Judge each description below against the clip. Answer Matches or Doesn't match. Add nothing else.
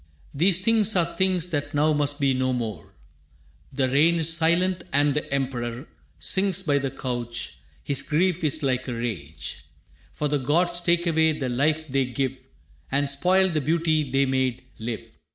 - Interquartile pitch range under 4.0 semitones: Doesn't match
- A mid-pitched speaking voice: Matches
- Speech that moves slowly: Doesn't match